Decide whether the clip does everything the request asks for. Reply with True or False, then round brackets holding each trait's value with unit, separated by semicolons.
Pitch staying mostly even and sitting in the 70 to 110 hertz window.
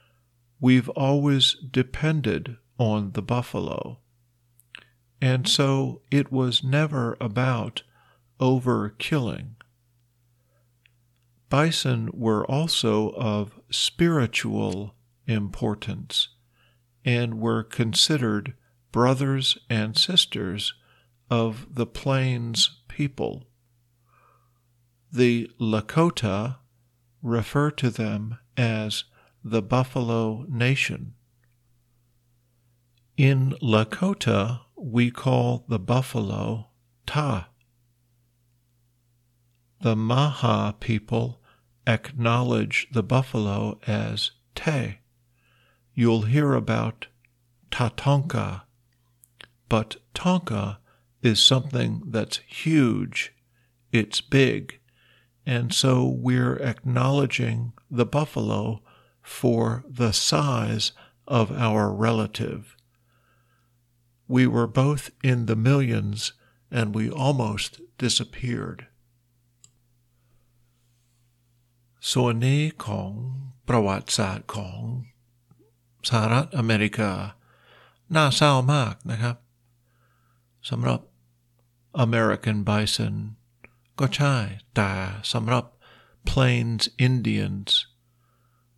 False (1.9 semitones; 120 Hz)